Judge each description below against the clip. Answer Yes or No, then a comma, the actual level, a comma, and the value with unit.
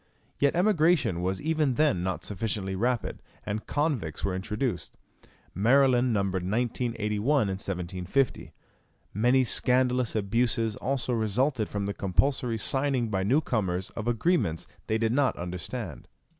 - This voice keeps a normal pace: No, slow, 130 wpm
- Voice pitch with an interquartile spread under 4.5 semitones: No, average, 5.1 semitones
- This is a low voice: Yes, low, 115 Hz